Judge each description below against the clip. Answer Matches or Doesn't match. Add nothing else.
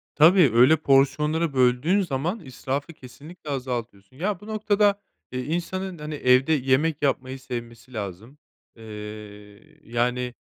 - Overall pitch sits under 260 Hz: Matches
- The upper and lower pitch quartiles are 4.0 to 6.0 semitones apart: Matches